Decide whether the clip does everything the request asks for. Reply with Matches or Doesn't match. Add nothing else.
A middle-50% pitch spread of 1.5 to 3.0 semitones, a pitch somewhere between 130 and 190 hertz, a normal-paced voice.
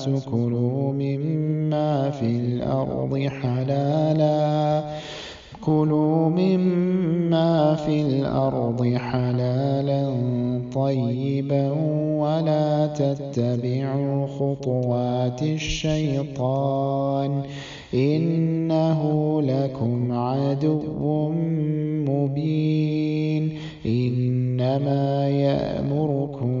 Doesn't match